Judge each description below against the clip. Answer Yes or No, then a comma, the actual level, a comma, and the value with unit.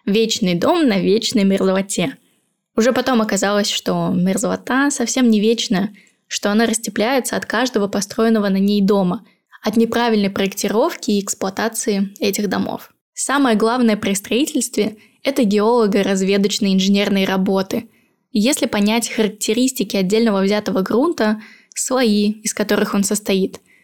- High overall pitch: Yes, high, 215 Hz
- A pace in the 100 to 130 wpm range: Yes, average, 125 wpm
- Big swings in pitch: No, narrow, 2.6 semitones